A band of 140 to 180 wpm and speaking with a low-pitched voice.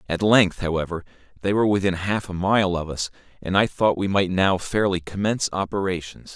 No: average, 190 wpm; very low, 95 Hz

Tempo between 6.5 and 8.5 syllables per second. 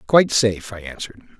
Yes: 7.0 syllables/s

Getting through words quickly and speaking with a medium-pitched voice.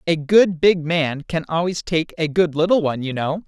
Yes: fast, 225 wpm; medium, 165 Hz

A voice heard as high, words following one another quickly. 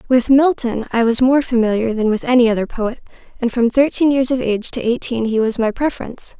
Yes: high, 240 Hz; fast, 215 wpm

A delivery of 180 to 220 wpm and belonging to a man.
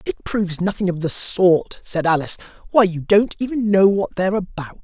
Yes: average, 200 wpm; male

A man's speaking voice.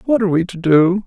Yes: male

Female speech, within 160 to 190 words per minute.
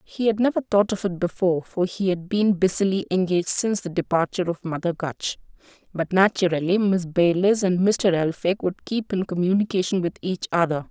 Yes: female; average, 180 wpm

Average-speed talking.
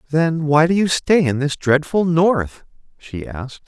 Yes: average, 180 wpm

